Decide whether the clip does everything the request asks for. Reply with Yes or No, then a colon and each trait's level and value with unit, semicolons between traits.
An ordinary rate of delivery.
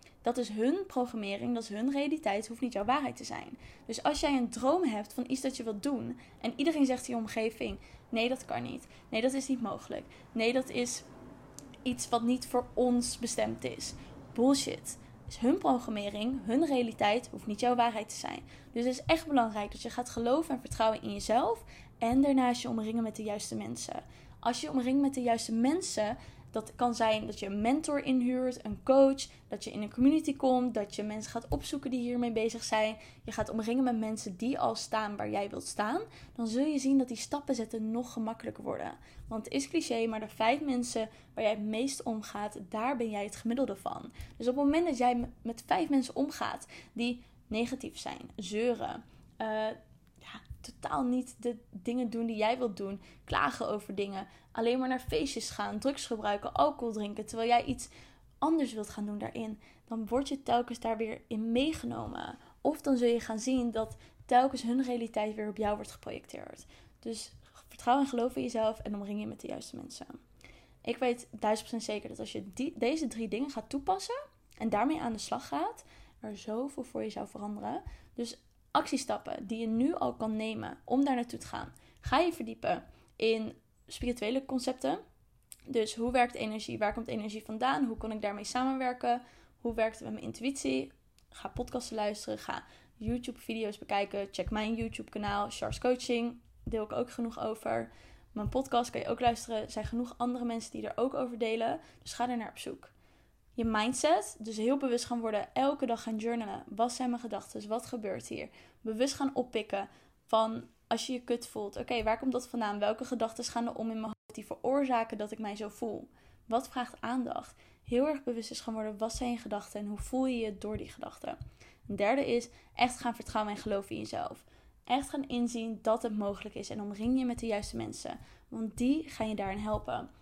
No: fast, 205 wpm